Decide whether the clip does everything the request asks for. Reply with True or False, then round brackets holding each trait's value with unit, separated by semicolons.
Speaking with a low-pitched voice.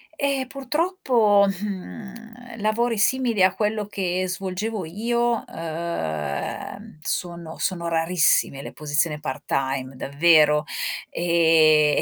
False (185 Hz)